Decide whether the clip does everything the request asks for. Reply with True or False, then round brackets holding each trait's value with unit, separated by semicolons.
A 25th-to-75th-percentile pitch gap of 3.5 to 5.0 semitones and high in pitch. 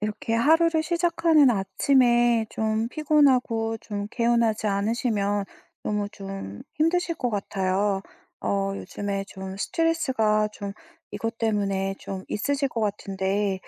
True (4.4 semitones; 220 Hz)